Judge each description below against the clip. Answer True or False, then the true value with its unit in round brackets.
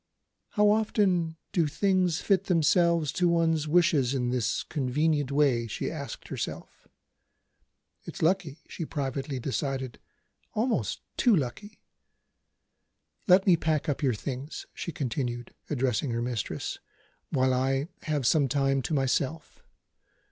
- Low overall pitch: False (145 Hz)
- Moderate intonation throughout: True (4.4 semitones)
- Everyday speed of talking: False (125 wpm)